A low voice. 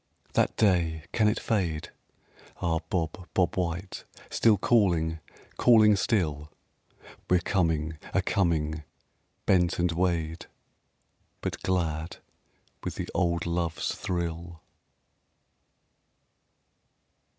Yes: very low, 85 Hz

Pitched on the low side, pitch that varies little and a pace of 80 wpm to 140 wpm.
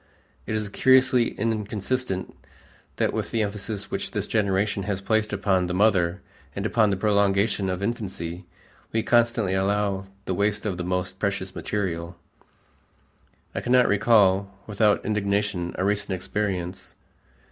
Yes: low, 100 Hz; narrow, 2.2 semitones; slow, 135 wpm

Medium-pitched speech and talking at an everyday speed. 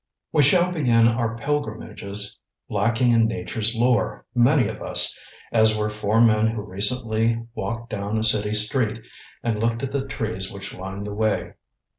No: low, 110 Hz; average, 160 wpm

